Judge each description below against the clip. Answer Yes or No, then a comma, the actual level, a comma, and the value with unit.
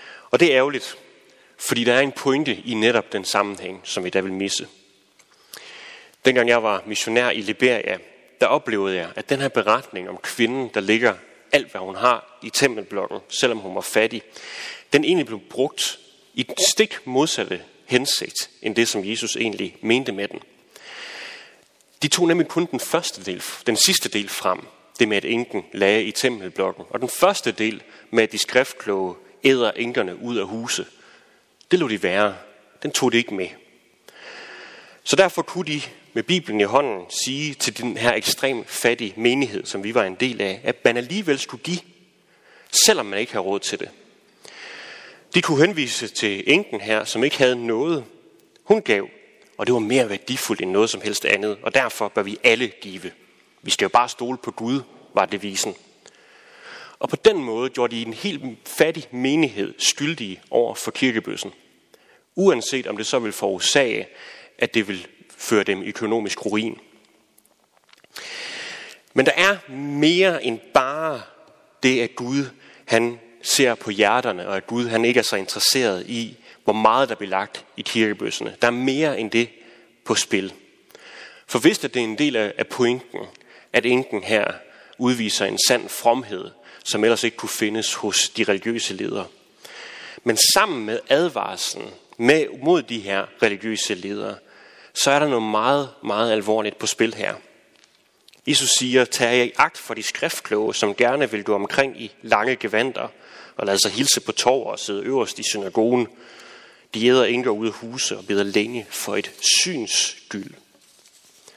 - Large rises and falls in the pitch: No, average, 4.3 semitones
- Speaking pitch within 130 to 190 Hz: No, low, 120 Hz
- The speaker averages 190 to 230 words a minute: No, average, 170 wpm